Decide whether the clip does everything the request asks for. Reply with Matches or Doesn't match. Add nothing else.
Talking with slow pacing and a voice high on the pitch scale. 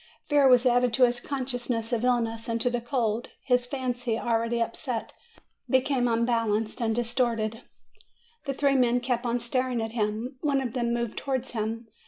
Doesn't match